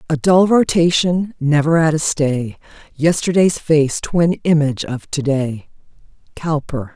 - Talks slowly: Yes, slow, 130 wpm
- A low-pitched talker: No, medium, 155 Hz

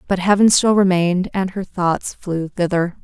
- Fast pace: No, average, 180 wpm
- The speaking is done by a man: No, female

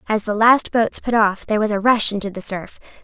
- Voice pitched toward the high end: Yes, high, 215 Hz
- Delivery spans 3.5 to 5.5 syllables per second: No, 5.7 syllables/s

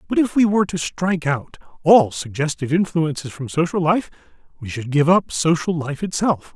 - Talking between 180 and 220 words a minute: Yes, average, 185 wpm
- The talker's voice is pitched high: No, medium, 160 Hz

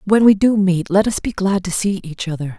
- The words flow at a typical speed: No, fast, 280 wpm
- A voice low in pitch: No, high, 190 Hz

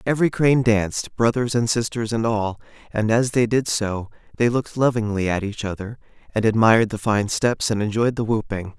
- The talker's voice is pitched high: No, low, 110 Hz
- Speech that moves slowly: No, average, 190 wpm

